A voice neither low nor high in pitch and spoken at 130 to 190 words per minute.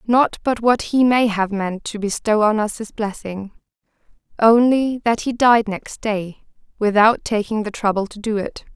No: high, 215 Hz; average, 180 wpm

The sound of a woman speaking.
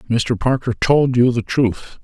No: male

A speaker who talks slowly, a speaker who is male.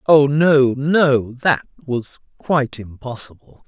Yes: slow, 115 wpm; male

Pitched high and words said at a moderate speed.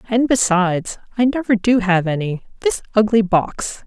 Yes: high, 205 Hz; average, 155 wpm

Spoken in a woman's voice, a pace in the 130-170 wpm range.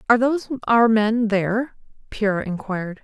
Yes: female; average, 140 wpm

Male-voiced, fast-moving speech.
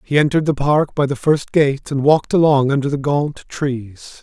Yes: male; fast, 215 wpm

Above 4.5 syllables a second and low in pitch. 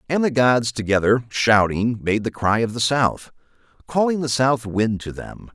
No: 4.4 syllables/s; low, 120 Hz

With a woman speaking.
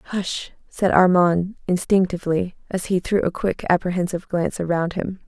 Yes: female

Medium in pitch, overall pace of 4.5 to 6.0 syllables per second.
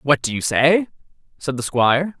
Yes: medium, 145 Hz; 4.9 syllables/s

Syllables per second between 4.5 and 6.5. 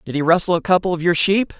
No: 6.8 syllables/s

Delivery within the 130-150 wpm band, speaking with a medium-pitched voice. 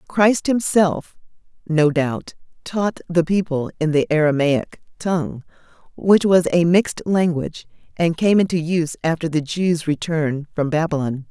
Yes: average, 140 wpm; medium, 165 Hz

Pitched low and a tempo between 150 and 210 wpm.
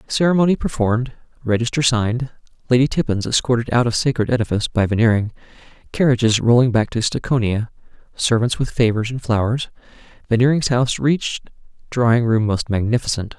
No: low, 120 Hz; slow, 135 wpm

